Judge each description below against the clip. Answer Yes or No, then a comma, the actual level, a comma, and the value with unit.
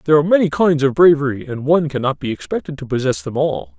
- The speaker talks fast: Yes, fast, 240 wpm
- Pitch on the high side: No, medium, 140 Hz